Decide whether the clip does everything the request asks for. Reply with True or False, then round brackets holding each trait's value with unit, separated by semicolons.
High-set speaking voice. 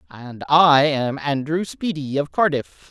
False (150 Hz)